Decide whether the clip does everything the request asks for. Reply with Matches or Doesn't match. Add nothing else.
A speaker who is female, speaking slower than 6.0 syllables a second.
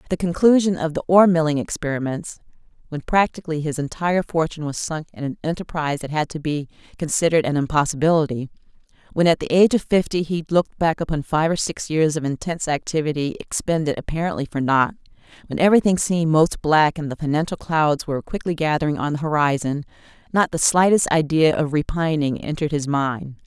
Doesn't match